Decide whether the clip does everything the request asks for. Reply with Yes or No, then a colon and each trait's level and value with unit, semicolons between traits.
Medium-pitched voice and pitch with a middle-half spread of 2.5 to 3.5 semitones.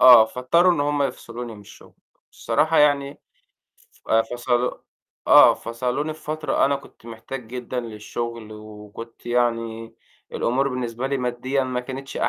No: low, 125 Hz; average, 3.0 semitones